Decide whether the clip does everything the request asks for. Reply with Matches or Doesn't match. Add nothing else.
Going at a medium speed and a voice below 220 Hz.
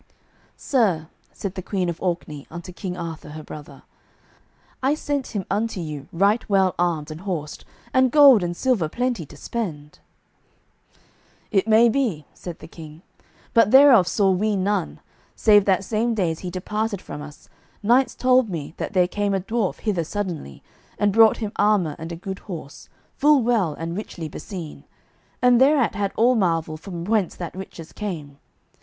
Matches